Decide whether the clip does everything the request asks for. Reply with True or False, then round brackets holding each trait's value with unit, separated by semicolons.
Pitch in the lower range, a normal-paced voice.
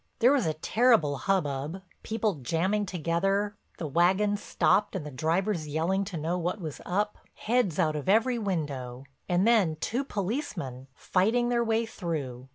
False (185 Hz; 160 wpm)